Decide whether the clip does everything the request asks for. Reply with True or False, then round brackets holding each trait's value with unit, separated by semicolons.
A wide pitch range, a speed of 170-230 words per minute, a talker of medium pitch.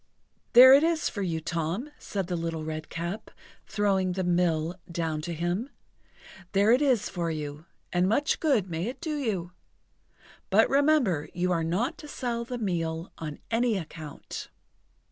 False (6.2 semitones; 160 wpm; 180 Hz)